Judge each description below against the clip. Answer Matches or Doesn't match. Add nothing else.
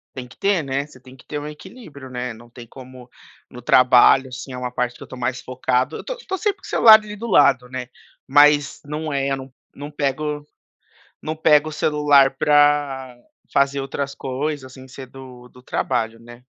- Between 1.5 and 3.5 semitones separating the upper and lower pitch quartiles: Matches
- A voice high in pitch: Doesn't match